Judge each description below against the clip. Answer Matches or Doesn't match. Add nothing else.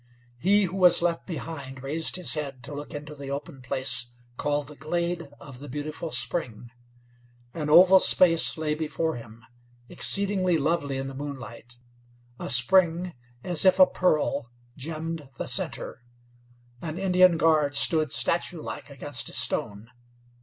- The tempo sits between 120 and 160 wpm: Matches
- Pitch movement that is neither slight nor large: Matches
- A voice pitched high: Doesn't match